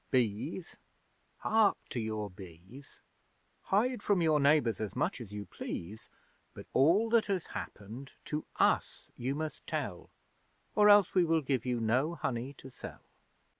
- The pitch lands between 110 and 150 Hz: Yes, low, 135 Hz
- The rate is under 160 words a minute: Yes, average, 150 wpm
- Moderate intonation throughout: No, wide, 7.5 semitones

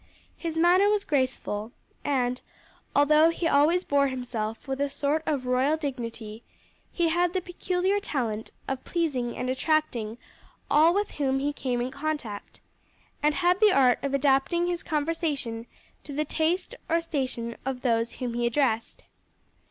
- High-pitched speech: Yes, very high, 280 Hz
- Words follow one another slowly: No, average, 150 wpm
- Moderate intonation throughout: Yes, average, 4.8 semitones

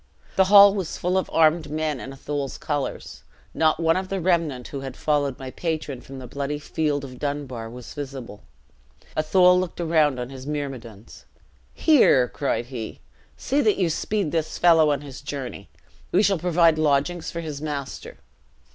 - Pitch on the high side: No, medium, 150 Hz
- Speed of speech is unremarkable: Yes, average, 170 wpm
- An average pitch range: Yes, average, 3.8 semitones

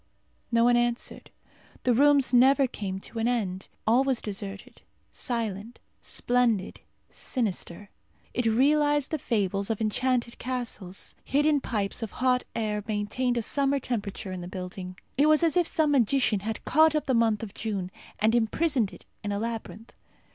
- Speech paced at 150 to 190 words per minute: Yes, average, 160 wpm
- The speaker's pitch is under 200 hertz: No, high, 235 Hz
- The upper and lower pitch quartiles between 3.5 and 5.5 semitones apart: Yes, average, 4.1 semitones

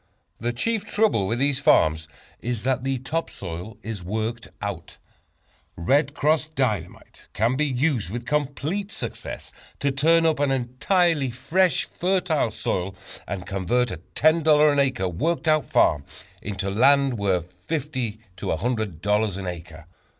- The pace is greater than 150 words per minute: No, average, 145 wpm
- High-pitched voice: No, low, 125 Hz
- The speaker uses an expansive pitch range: Yes, wide, 7.0 semitones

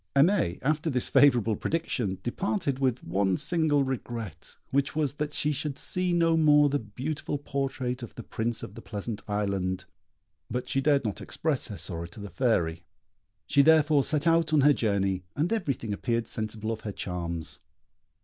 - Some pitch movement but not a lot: No, wide, 6.3 semitones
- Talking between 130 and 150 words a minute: No, average, 170 wpm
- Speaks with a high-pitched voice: No, low, 130 Hz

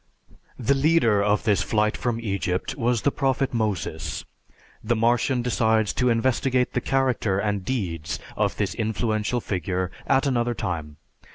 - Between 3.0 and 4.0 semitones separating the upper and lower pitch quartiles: Yes, average, 3.7 semitones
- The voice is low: Yes, low, 115 Hz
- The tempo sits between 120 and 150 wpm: Yes, average, 145 wpm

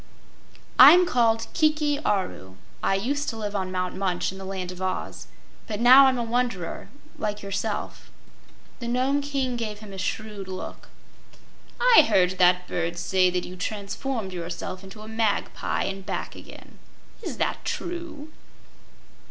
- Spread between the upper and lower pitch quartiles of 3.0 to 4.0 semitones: No, average, 5.2 semitones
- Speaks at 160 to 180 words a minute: No, average, 150 wpm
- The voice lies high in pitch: Yes, high, 210 Hz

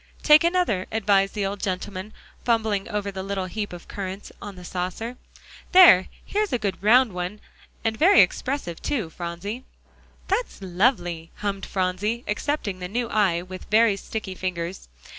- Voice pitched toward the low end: No, high, 200 Hz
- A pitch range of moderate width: Yes, average, 3.7 semitones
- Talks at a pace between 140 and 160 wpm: Yes, average, 155 wpm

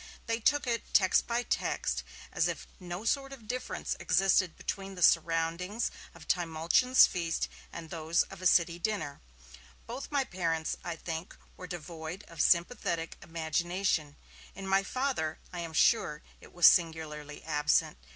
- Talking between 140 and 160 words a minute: Yes, average, 150 wpm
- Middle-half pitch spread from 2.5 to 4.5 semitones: Yes, average, 3.4 semitones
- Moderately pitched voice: Yes, medium, 175 Hz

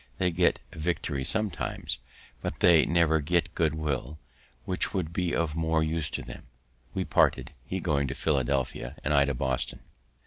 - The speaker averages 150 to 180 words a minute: Yes, average, 165 wpm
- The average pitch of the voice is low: Yes, very low, 80 Hz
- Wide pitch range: No, average, 3.4 semitones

